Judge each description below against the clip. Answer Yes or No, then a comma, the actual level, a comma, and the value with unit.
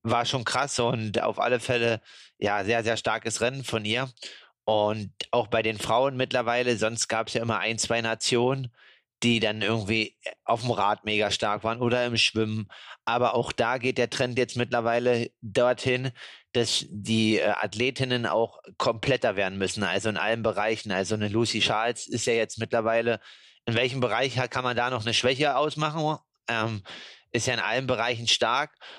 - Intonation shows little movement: Yes, narrow, 2.0 semitones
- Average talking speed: Yes, average, 175 wpm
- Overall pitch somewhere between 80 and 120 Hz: Yes, low, 115 Hz